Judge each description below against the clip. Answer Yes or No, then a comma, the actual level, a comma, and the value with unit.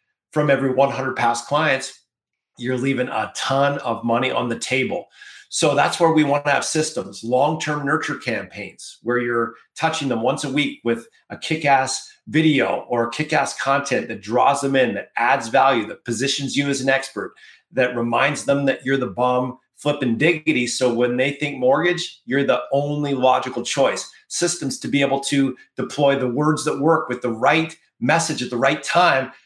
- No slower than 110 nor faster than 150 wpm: No, average, 185 wpm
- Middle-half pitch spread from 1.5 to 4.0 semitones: Yes, average, 2.9 semitones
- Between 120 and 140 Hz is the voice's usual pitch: Yes, low, 135 Hz